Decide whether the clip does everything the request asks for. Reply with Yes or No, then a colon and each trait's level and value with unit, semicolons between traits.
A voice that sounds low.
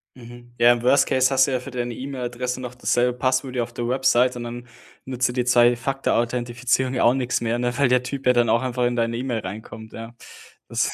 Yes: low, 125 Hz